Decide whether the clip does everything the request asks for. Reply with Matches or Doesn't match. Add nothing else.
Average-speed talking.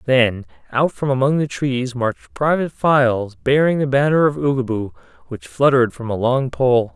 Matches